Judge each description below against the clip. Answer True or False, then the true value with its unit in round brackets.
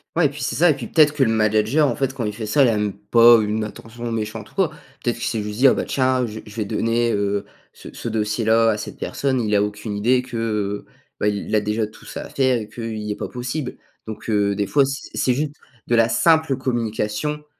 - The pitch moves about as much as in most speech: True (3.5 semitones)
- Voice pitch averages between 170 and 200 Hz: False (115 Hz)